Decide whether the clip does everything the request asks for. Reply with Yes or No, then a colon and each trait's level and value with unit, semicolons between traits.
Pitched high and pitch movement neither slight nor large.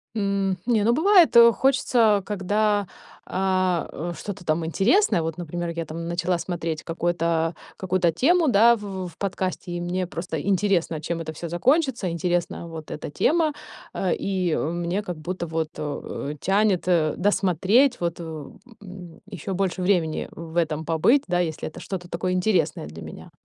No: medium, 180 Hz; average, 3.3 semitones